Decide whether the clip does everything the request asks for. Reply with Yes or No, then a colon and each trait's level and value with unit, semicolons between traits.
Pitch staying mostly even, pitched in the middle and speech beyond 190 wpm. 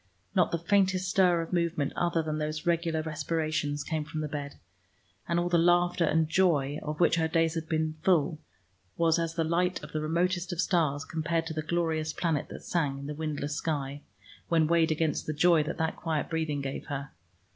Yes: narrow, 1.8 semitones; medium, 160 Hz; average, 200 wpm